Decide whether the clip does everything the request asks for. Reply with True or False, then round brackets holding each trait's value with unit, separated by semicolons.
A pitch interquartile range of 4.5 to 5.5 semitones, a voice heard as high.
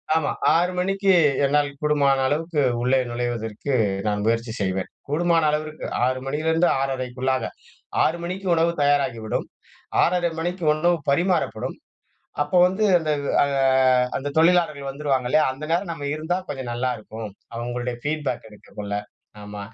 False (5.0 semitones; 145 Hz)